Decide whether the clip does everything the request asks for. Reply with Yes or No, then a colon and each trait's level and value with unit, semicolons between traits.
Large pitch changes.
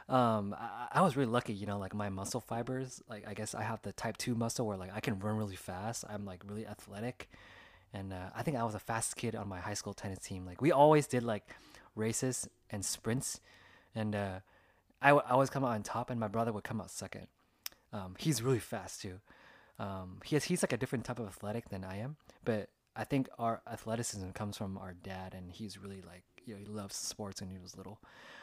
No: average, 3.7 semitones